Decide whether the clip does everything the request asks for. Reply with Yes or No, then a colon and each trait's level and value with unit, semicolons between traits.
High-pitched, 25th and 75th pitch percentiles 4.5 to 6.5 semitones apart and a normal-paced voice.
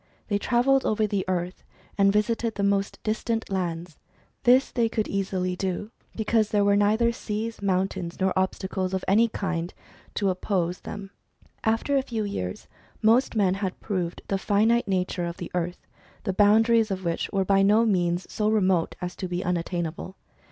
No: high, 195 Hz; average, 3.0 semitones; average, 170 wpm